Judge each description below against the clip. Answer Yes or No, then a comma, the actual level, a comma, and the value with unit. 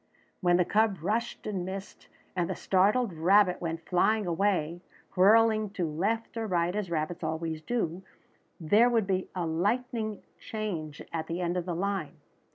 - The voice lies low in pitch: No, medium, 185 Hz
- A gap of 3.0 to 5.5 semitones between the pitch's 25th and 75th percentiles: Yes, average, 4.0 semitones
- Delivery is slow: No, average, 165 wpm